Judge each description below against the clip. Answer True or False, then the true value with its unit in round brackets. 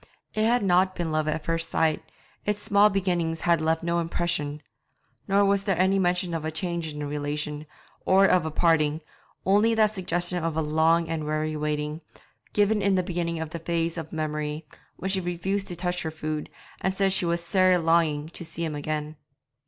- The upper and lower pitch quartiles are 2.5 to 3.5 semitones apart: True (3.1 semitones)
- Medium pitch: True (170 Hz)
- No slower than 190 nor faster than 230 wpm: True (200 wpm)